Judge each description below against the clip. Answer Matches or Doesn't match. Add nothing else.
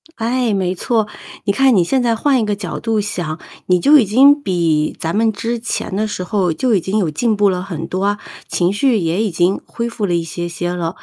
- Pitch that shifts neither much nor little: Matches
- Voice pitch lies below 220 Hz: Matches